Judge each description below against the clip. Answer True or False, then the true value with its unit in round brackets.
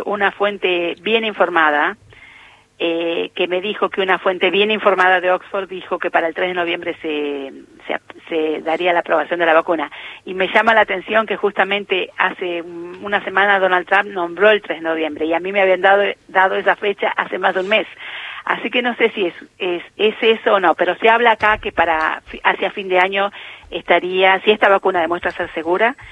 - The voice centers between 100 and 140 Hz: False (190 Hz)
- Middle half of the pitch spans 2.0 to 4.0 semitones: True (2.7 semitones)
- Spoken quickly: True (205 wpm)